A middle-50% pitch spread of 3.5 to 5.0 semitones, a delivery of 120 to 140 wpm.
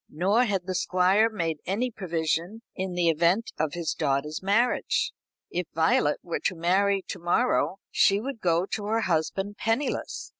No: average, 4.1 semitones; average, 160 wpm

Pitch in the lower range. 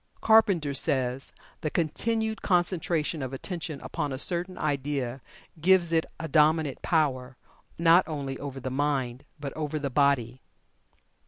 No: medium, 150 Hz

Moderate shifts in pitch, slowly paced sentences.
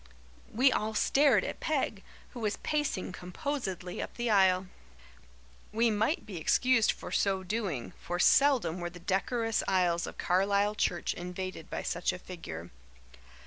No: average, 4.3 semitones; average, 145 wpm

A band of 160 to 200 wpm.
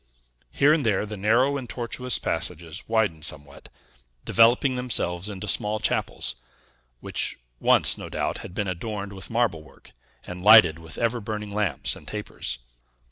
No: average, 150 wpm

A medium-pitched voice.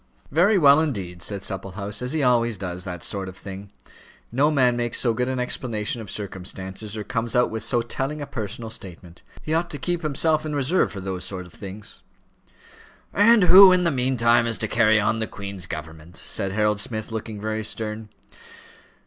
No: low, 110 Hz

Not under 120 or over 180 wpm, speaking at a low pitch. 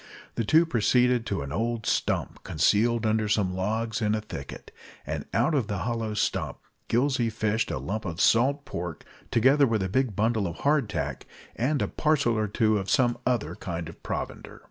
No: average, 195 wpm; low, 110 Hz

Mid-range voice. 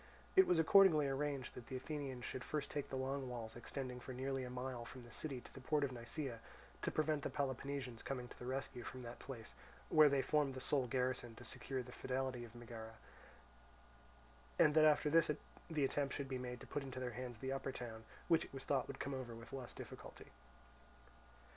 No: low, 130 Hz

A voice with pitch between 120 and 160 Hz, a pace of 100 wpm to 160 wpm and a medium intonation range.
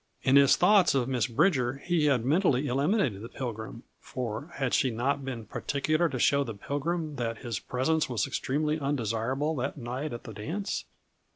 No: low, 135 Hz; average, 175 wpm; average, 4.0 semitones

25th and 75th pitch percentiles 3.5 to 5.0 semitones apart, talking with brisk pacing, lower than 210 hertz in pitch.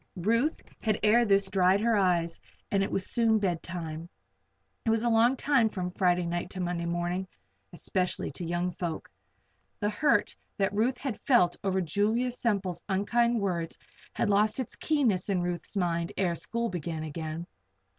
No: average, 4.3 semitones; average, 165 wpm; high, 190 Hz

